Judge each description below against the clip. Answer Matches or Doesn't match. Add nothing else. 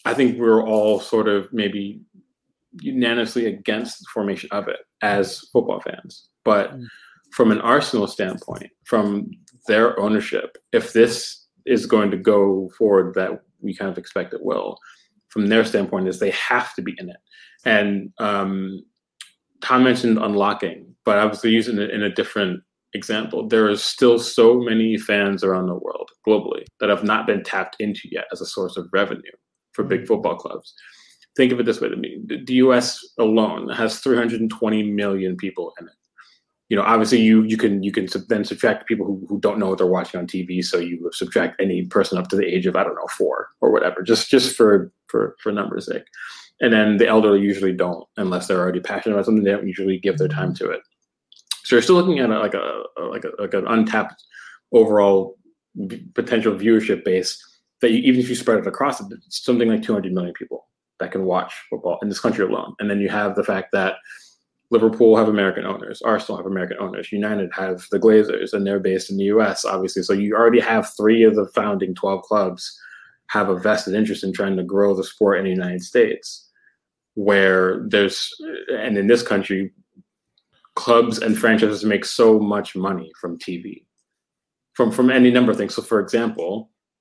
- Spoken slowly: Doesn't match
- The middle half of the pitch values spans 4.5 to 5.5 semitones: Doesn't match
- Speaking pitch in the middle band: Doesn't match